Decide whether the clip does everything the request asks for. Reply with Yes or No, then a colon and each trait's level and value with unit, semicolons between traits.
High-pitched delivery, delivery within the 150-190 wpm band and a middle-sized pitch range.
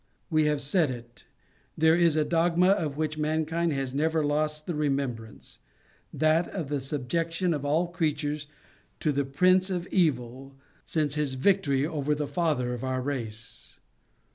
No: medium, 150 Hz; average, 160 wpm; average, 3.2 semitones